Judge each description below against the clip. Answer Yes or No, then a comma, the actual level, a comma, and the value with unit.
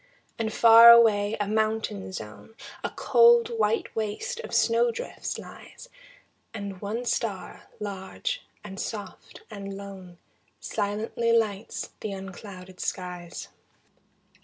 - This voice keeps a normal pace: No, slow, 110 wpm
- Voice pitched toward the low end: No, high, 210 Hz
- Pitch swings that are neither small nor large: Yes, average, 3.1 semitones